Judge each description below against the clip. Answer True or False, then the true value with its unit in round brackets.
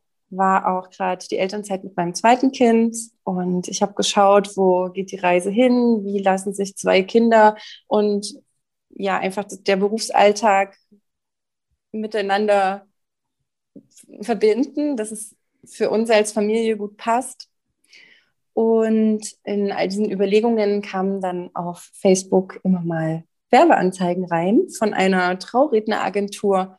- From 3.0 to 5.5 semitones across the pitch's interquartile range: False (2.5 semitones)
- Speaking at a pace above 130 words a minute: False (125 wpm)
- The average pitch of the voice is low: False (205 Hz)